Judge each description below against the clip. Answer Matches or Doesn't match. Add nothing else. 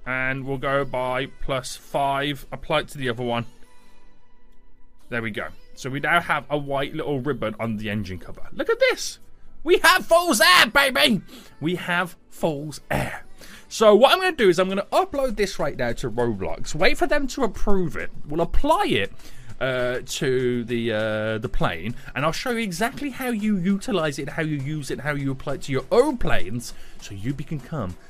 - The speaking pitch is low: Doesn't match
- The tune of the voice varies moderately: Doesn't match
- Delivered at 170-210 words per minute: Matches